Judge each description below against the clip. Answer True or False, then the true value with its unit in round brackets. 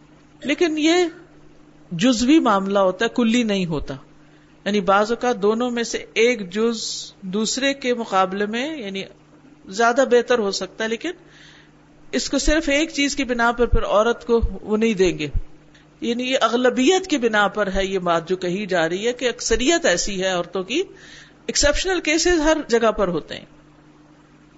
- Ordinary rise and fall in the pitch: False (6.2 semitones)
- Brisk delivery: False (175 wpm)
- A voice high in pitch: True (230 Hz)